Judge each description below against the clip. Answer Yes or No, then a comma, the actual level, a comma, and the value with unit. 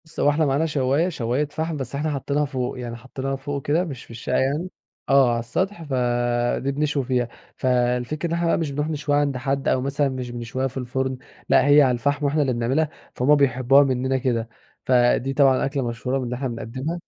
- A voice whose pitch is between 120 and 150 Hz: Yes, low, 135 Hz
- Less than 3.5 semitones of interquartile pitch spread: Yes, average, 2.8 semitones